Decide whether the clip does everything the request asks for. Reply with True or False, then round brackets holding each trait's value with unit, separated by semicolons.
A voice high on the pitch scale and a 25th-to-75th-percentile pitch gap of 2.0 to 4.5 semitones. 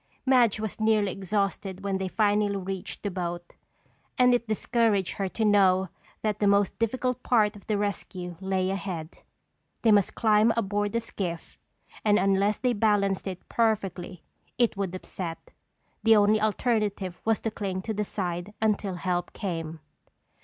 True (200 Hz; 2.4 semitones)